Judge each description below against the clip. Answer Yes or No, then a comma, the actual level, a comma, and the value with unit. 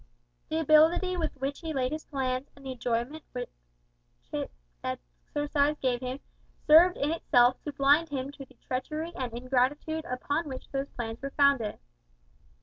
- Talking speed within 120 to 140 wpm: No, average, 155 wpm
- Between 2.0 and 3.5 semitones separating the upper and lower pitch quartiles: Yes, average, 3.2 semitones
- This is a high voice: Yes, very high, 275 Hz